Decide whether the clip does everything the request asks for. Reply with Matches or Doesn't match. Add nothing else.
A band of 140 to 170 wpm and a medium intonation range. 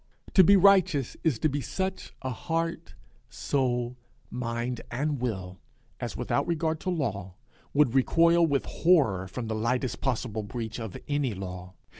Doesn't match